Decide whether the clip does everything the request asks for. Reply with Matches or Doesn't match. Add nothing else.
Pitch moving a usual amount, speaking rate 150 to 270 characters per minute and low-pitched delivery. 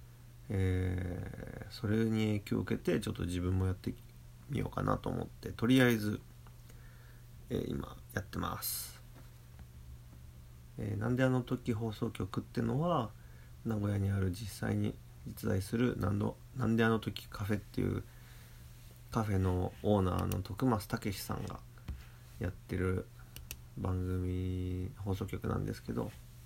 Matches